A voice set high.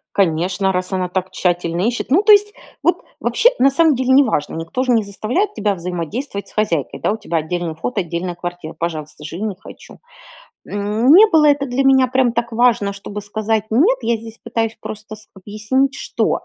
Yes: high, 215 Hz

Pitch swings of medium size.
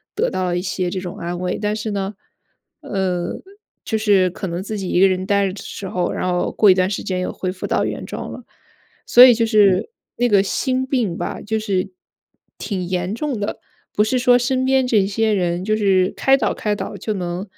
Yes: average, 3.1 semitones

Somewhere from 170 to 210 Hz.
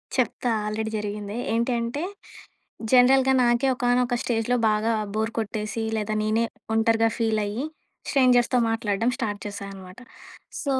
No: high, 225 Hz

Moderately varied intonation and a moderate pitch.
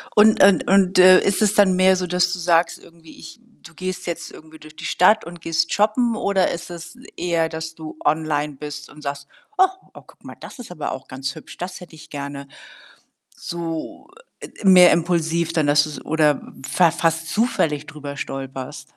Yes: average, 3.2 semitones; medium, 165 Hz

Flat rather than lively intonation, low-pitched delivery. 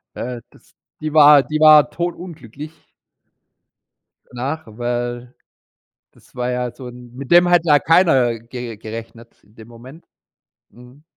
No: average, 4.2 semitones; low, 125 Hz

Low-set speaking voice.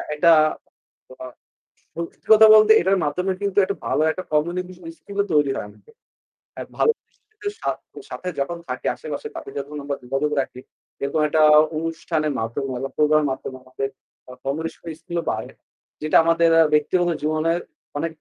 No: medium, 155 Hz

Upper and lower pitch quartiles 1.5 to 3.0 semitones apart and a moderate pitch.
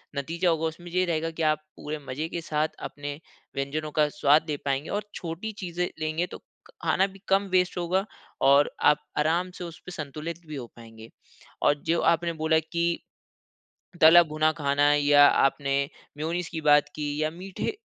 Yes: average, 2.7 semitones; medium, 155 Hz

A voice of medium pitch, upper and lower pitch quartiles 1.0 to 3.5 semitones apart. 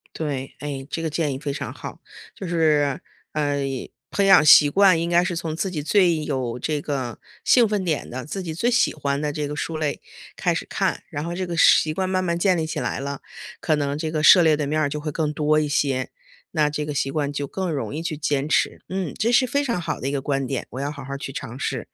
Yes: medium, 150 Hz; average, 3.1 semitones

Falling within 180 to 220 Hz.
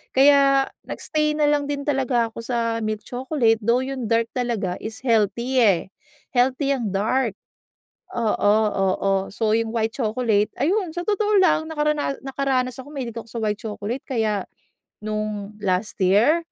No: high, 235 Hz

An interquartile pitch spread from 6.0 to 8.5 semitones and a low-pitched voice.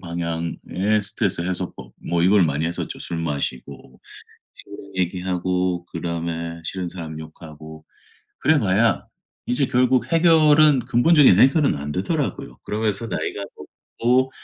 Yes: wide, 6.3 semitones; very low, 90 Hz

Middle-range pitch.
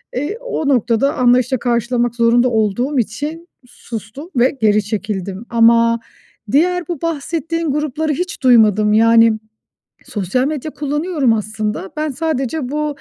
No: very high, 250 Hz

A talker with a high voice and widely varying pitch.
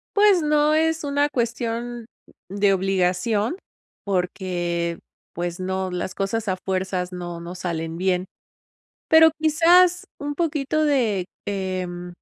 Yes: high, 195 Hz; wide, 8.3 semitones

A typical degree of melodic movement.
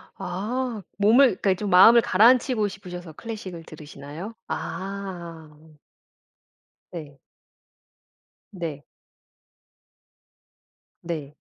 Yes: average, 4.5 semitones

